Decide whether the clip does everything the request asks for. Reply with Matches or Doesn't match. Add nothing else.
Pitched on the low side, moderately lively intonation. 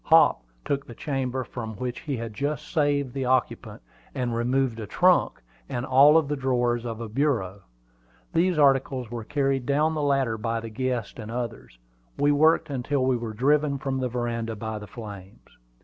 Matches